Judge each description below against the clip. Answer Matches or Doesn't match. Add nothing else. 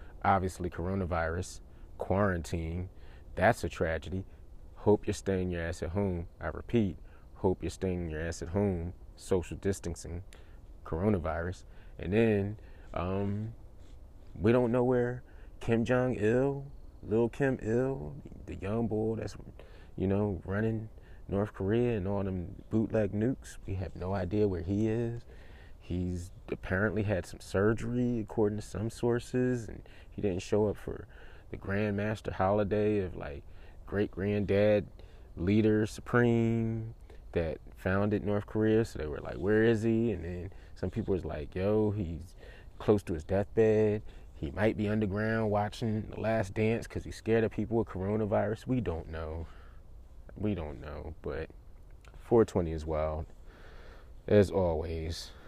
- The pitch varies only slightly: Doesn't match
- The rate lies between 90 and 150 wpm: Matches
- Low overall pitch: Matches